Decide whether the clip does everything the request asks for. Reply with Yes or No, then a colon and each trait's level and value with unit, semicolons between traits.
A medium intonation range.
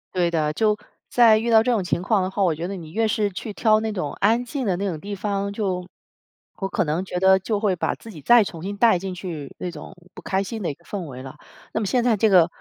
Yes: average, 3.7 semitones